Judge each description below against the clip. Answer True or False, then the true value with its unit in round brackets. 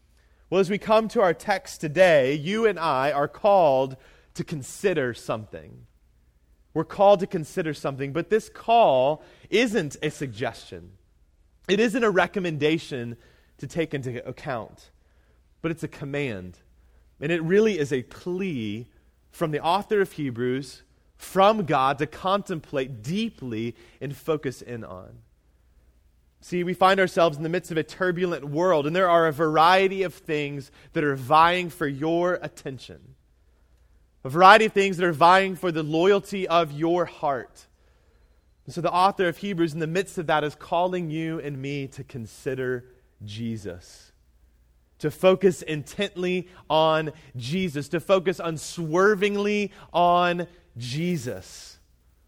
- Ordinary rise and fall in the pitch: False (7.8 semitones)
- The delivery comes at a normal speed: True (145 wpm)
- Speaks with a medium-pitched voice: True (155 Hz)